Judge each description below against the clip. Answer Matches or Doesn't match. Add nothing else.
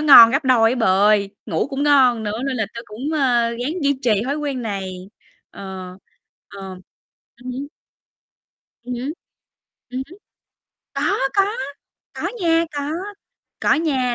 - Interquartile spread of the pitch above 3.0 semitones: Matches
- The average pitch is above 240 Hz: Matches